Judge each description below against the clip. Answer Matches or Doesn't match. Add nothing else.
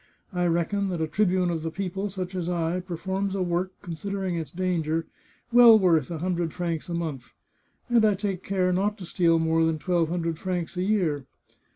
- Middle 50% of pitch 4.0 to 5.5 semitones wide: Doesn't match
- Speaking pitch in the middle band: Matches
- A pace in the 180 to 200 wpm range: Matches